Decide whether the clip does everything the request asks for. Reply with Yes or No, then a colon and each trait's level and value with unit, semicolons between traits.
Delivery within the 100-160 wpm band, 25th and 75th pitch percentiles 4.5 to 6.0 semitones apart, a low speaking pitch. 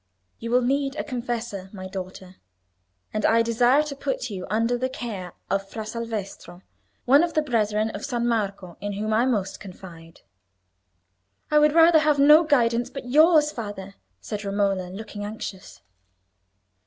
No: average, 155 wpm; average, 4.8 semitones; high, 225 Hz